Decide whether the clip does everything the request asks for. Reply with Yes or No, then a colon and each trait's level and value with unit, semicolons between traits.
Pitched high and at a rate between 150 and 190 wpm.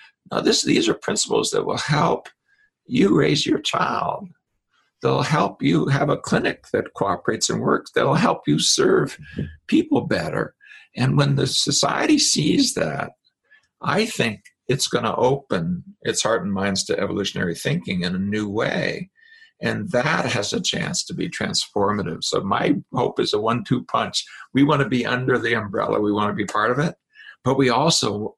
No: medium, 150 Hz; average, 180 wpm